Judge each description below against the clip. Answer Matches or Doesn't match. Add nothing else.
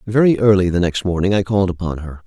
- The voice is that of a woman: Doesn't match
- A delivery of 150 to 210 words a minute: Doesn't match